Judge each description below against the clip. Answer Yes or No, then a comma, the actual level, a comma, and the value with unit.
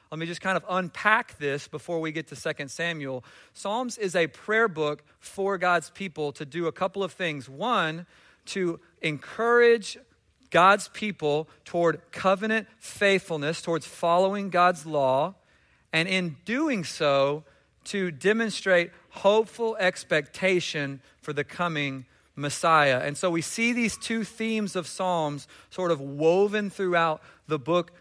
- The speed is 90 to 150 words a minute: Yes, average, 140 wpm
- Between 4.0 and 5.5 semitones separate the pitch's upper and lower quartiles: Yes, average, 4.4 semitones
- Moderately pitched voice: Yes, medium, 175 Hz